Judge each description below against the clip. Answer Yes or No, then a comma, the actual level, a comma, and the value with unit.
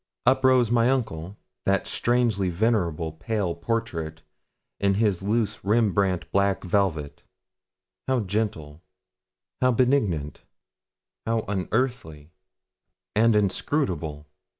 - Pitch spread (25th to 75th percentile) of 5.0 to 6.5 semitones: Yes, wide, 5.4 semitones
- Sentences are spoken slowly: Yes, slow, 95 wpm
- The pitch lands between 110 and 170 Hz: No, low, 100 Hz